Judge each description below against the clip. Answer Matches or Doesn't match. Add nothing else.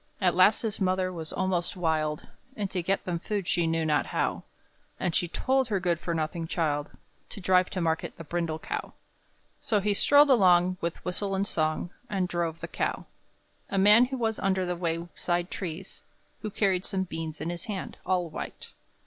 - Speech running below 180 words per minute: Doesn't match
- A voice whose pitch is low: Doesn't match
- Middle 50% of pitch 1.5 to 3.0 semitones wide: Matches